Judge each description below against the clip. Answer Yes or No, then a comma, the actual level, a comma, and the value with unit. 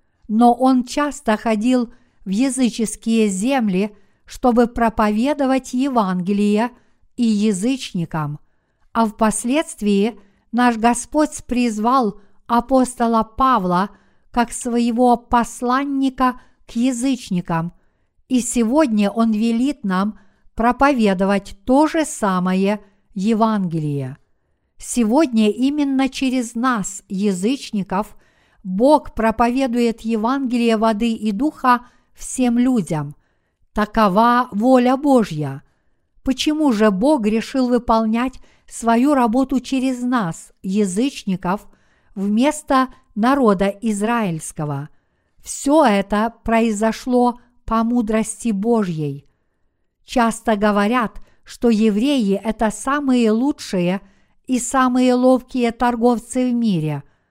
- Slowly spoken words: Yes, slow, 85 wpm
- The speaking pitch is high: Yes, high, 230 Hz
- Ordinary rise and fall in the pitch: Yes, average, 3.5 semitones